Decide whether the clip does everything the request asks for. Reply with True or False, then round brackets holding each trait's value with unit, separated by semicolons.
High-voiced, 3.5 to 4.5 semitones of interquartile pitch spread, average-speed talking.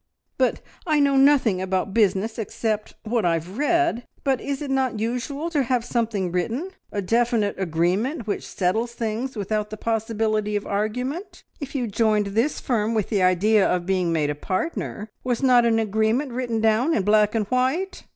True (225 Hz; 3.8 semitones; 180 wpm)